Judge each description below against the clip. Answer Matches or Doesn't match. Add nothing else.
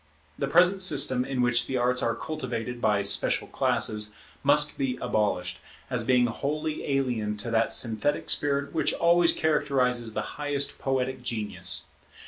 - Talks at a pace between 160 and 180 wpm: Doesn't match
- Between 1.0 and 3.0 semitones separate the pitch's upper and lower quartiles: Doesn't match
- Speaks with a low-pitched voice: Matches